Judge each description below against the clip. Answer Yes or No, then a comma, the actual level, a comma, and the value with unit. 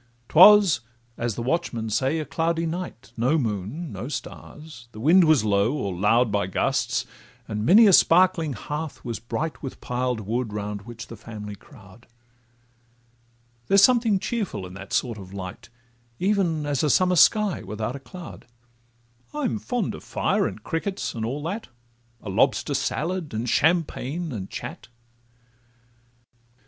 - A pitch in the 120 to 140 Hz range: Yes, low, 135 Hz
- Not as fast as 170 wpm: Yes, average, 155 wpm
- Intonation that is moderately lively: No, wide, 7.7 semitones